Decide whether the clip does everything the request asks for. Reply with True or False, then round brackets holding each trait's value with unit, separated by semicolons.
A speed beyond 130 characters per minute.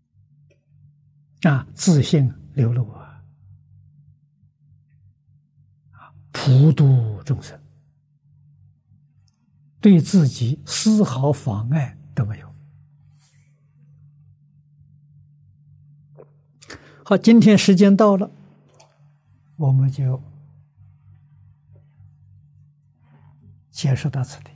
False (90 characters per minute)